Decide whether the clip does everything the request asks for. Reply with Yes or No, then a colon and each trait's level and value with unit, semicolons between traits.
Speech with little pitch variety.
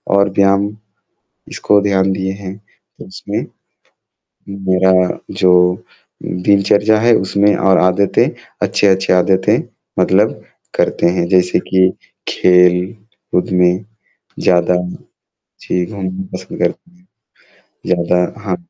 Yes: narrow, 1.7 semitones